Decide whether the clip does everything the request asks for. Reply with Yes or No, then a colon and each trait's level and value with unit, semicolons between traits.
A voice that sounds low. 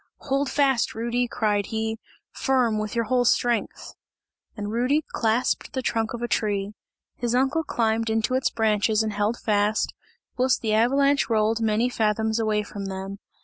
No: high, 225 Hz